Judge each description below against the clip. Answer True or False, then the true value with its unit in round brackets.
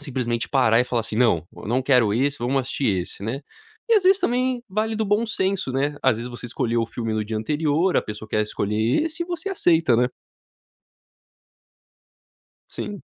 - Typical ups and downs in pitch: False (8.9 semitones)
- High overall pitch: False (130 Hz)